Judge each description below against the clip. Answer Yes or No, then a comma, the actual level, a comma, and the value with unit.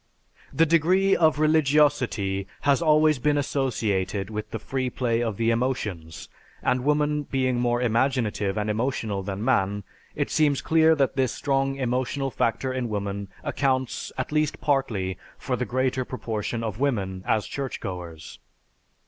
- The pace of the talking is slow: No, average, 145 wpm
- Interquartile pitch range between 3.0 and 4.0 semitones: No, average, 4.9 semitones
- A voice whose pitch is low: Yes, low, 125 Hz